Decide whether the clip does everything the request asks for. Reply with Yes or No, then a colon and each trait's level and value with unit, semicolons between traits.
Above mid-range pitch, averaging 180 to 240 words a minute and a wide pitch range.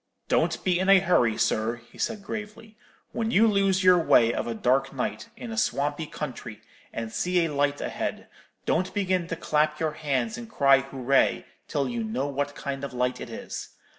No: medium, 150 Hz; average, 195 wpm; wide, 6.0 semitones